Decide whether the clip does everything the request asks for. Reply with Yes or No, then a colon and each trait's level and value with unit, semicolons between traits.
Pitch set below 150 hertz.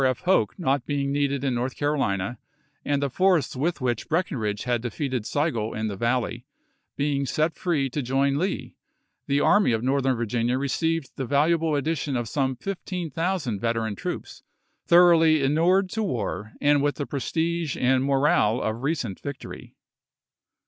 Yes: medium, 140 Hz